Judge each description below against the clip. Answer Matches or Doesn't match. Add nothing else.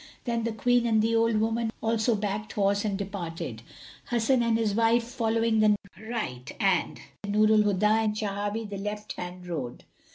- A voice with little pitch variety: Matches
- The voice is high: Matches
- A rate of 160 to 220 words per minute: Matches